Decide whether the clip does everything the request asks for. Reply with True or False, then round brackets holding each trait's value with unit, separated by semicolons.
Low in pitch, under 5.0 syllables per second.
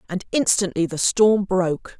False (190 Hz; 4.6 syllables/s)